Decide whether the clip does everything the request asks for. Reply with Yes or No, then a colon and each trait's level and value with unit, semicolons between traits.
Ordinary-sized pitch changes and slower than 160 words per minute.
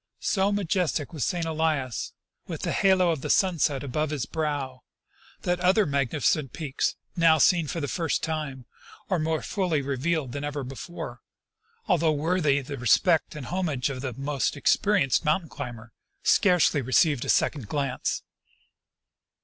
Yes: average, 3.9 semitones; average, 150 wpm